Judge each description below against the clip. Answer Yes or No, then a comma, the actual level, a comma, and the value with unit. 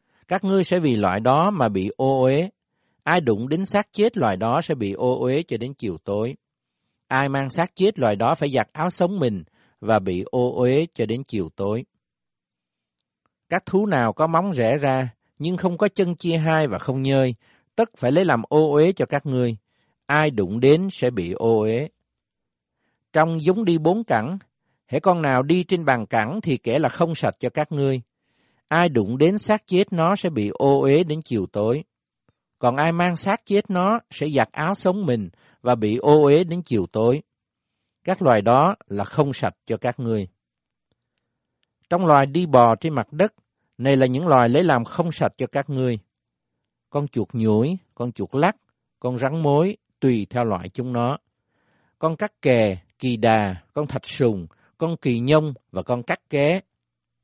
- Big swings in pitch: Yes, wide, 6.3 semitones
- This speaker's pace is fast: No, average, 190 wpm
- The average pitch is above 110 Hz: Yes, low, 135 Hz